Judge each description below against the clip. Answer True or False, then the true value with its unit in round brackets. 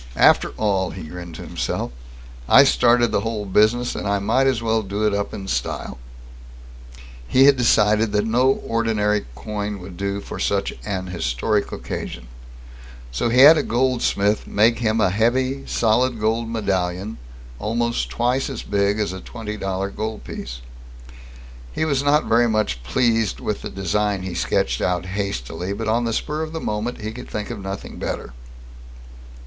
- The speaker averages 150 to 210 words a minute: True (170 wpm)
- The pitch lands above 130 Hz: False (105 Hz)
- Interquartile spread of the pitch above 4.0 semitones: False (3.1 semitones)